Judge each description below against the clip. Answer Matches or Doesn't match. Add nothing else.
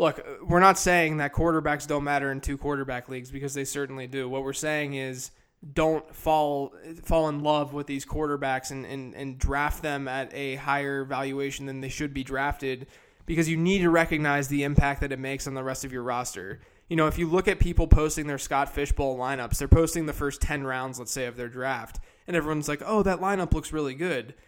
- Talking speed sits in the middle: Doesn't match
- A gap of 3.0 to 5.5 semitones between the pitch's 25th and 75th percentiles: Doesn't match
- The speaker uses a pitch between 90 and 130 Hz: Doesn't match